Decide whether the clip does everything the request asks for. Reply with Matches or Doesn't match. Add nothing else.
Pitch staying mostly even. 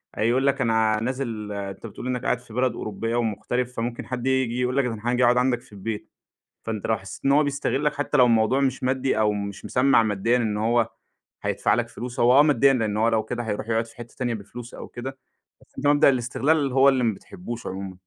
Doesn't match